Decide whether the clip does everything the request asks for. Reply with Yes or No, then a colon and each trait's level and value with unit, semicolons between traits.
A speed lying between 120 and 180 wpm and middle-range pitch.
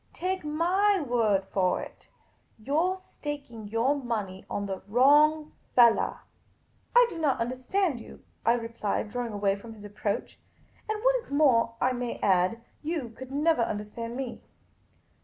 No: average, 160 wpm; high, 245 Hz